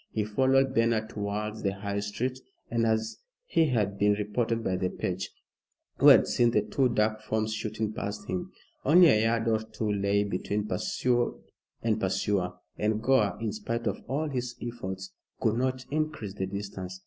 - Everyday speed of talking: Yes, average, 165 wpm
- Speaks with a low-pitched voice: Yes, low, 110 Hz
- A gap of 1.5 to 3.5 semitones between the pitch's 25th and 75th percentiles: Yes, average, 2.7 semitones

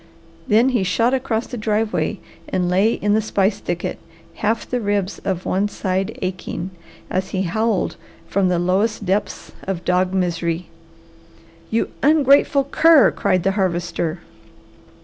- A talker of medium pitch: No, high, 195 Hz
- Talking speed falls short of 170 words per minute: Yes, average, 140 wpm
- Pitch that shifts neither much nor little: Yes, average, 3.4 semitones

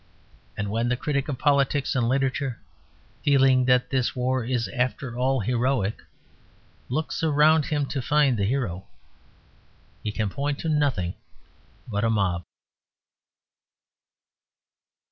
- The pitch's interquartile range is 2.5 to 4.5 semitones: Yes, average, 3.6 semitones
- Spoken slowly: Yes, slow, 125 wpm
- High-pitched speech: No, low, 130 Hz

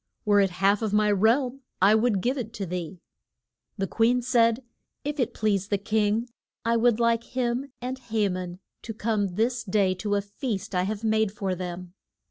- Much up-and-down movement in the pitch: No, average, 3.1 semitones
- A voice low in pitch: No, high, 215 Hz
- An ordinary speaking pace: Yes, average, 190 wpm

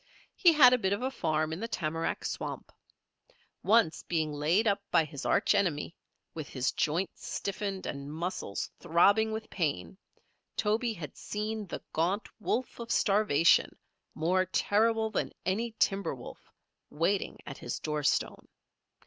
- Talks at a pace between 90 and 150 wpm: Yes, average, 145 wpm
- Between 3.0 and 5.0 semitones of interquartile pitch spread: No, wide, 5.6 semitones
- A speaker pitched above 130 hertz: Yes, high, 190 Hz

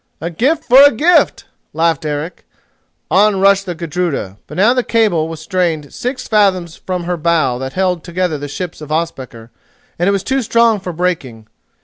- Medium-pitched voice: Yes, medium, 175 Hz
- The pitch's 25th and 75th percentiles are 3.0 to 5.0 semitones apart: Yes, average, 4.1 semitones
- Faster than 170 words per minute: Yes, average, 185 wpm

